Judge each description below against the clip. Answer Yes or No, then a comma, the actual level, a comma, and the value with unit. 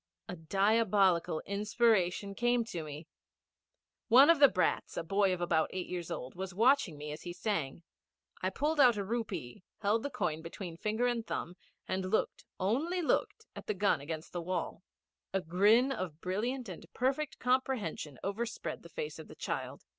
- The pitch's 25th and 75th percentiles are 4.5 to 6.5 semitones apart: Yes, wide, 5.4 semitones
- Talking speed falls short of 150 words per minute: No, average, 170 wpm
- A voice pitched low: No, high, 200 Hz